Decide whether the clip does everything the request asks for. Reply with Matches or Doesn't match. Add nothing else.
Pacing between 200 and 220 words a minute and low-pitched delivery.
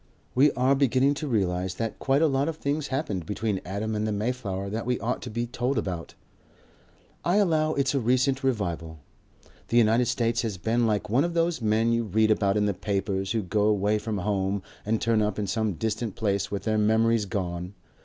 Matches